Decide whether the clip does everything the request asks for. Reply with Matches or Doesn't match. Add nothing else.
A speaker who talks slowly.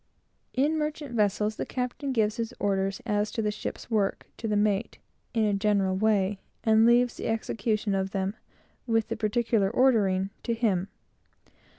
Doesn't match